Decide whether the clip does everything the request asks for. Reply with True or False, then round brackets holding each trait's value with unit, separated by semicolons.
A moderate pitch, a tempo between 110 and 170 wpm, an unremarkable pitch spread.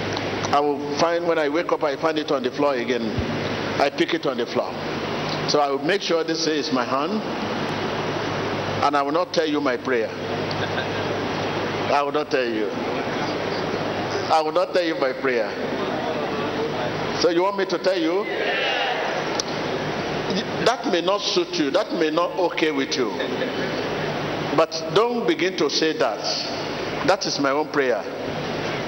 True (160 Hz; 160 wpm; 3.3 semitones)